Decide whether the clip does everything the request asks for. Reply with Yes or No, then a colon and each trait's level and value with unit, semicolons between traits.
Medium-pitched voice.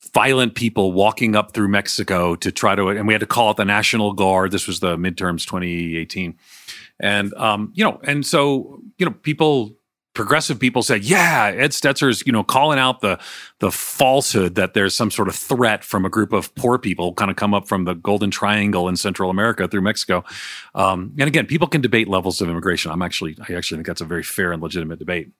No: low, 100 Hz